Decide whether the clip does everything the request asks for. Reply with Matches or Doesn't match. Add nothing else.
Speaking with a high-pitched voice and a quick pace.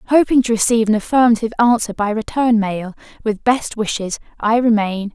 Doesn't match